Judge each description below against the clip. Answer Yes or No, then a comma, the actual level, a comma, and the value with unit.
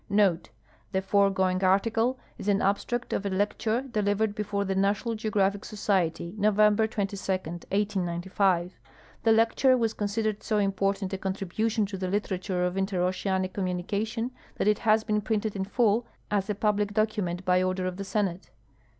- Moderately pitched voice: No, high, 200 Hz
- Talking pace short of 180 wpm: Yes, average, 155 wpm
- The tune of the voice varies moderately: No, narrow, 2.1 semitones